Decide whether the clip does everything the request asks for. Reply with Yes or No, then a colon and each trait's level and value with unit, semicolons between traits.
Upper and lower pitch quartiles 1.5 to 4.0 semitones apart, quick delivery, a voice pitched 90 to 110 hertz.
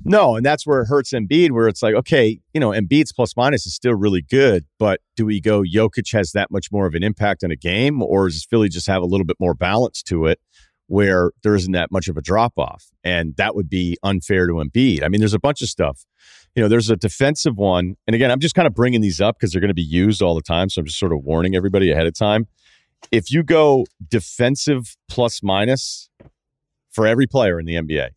No: average, 4.9 semitones; fast, 245 wpm; low, 105 Hz